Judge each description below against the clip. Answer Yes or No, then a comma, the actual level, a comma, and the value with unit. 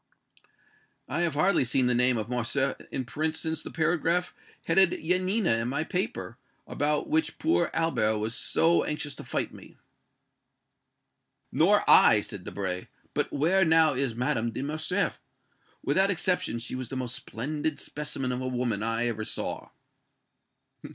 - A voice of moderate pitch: Yes, medium, 145 Hz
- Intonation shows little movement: No, average, 5.3 semitones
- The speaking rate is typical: Yes, average, 150 wpm